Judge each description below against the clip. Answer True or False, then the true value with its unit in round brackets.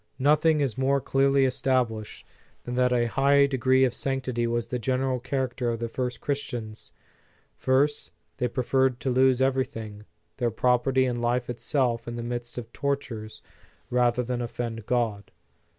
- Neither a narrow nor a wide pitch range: False (2.0 semitones)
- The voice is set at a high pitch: False (125 Hz)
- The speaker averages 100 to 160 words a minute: True (150 wpm)